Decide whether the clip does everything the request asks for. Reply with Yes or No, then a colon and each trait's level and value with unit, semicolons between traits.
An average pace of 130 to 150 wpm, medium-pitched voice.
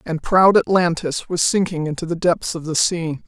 No: average, 200 wpm; medium, 170 Hz